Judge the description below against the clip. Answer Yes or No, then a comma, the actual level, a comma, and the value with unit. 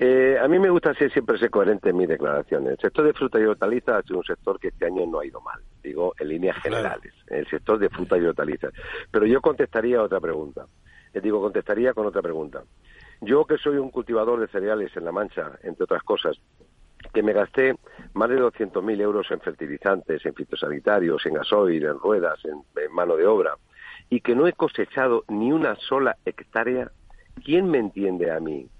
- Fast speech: Yes, fast, 200 wpm